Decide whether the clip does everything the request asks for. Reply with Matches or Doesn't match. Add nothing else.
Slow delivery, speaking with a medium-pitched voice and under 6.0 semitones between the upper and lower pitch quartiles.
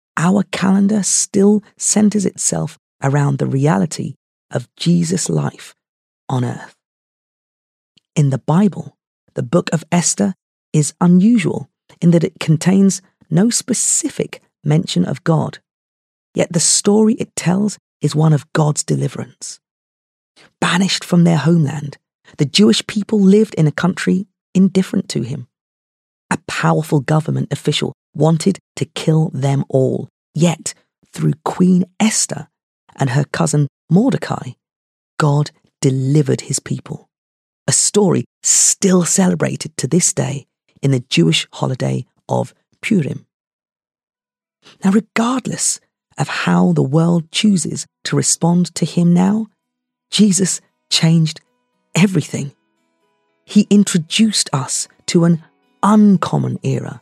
Matches